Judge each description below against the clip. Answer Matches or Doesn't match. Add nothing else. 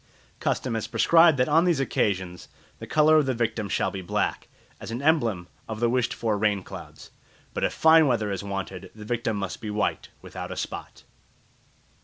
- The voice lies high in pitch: Doesn't match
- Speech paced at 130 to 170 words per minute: Doesn't match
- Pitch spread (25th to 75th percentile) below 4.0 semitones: Doesn't match